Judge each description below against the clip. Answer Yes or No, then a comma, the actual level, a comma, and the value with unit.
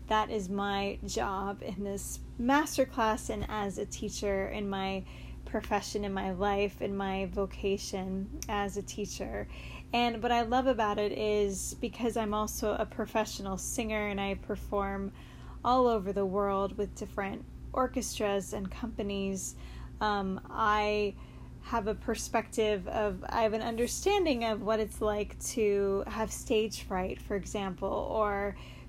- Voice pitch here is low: No, high, 210 Hz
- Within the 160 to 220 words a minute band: No, average, 145 wpm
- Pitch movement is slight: Yes, narrow, 1.9 semitones